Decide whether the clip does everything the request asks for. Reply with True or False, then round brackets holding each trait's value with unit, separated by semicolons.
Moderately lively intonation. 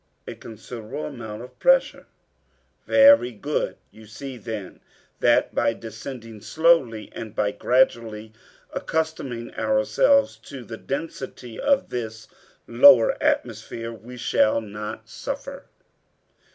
True (4.2 semitones)